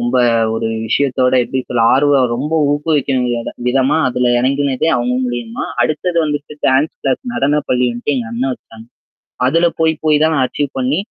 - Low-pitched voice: Yes, low, 130 Hz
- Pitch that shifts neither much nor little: Yes, average, 3.0 semitones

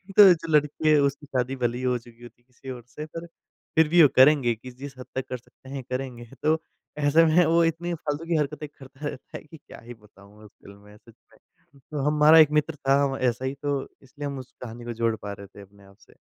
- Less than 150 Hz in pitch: Yes, low, 135 Hz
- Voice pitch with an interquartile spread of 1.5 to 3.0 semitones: No, average, 4.0 semitones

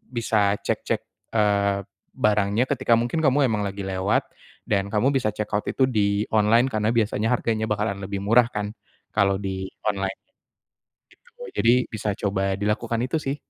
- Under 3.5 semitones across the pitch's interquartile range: Yes, narrow, 2.4 semitones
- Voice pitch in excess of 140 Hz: No, low, 105 Hz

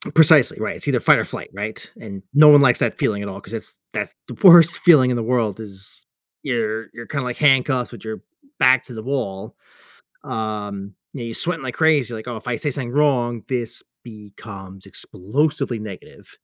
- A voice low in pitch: Yes, low, 120 Hz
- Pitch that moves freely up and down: No, average, 4.3 semitones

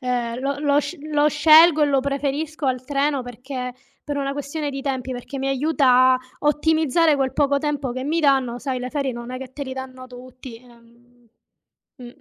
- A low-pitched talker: No, very high, 270 Hz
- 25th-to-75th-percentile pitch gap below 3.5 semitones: Yes, narrow, 2.5 semitones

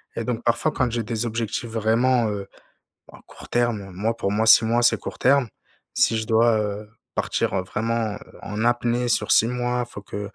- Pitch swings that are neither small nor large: No, narrow, 1.9 semitones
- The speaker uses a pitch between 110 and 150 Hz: Yes, low, 115 Hz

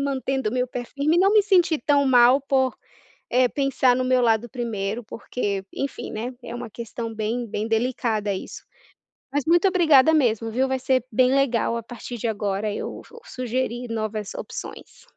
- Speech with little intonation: No, average, 3.3 semitones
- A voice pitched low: No, high, 245 Hz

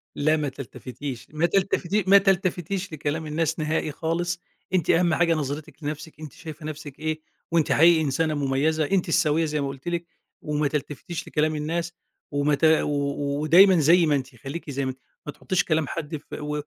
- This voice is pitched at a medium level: Yes, medium, 155 Hz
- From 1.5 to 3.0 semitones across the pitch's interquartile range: Yes, narrow, 2.5 semitones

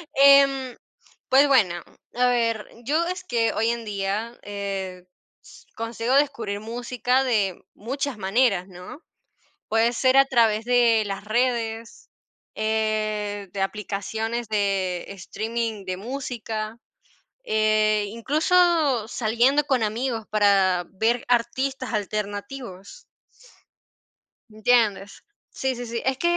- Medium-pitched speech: No, high, 225 Hz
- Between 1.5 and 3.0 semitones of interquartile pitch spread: No, average, 3.4 semitones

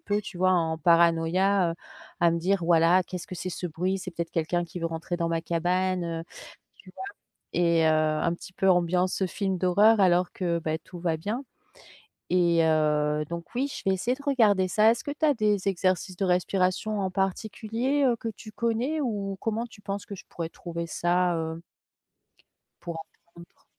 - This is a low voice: No, medium, 180 Hz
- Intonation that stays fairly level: No, average, 3.1 semitones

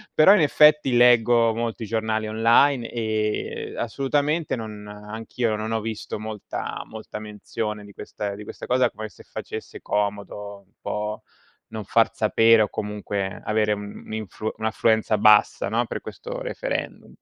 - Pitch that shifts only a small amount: Yes, narrow, 1.9 semitones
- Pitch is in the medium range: No, low, 110 Hz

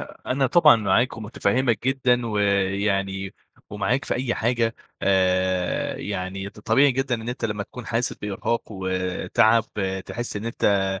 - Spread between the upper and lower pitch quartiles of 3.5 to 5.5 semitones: Yes, average, 3.9 semitones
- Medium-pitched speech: No, low, 110 Hz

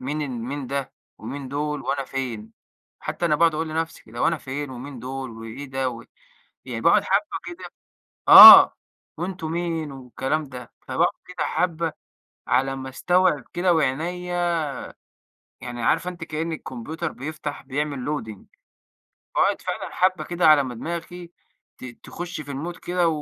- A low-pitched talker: No, medium, 150 Hz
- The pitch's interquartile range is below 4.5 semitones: Yes, average, 4.1 semitones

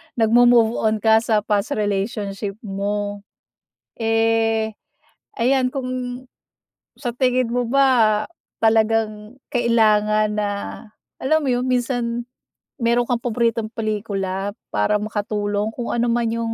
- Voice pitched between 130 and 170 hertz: No, high, 225 Hz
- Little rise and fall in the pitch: Yes, narrow, 2.3 semitones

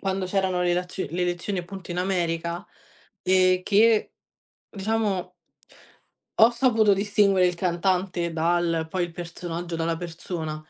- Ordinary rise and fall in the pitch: No, narrow, 2.2 semitones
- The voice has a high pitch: No, medium, 180 Hz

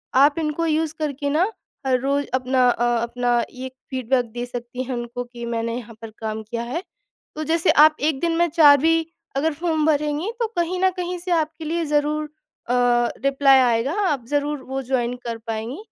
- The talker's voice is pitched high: Yes, very high, 275 Hz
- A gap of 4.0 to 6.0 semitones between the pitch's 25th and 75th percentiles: Yes, average, 4.3 semitones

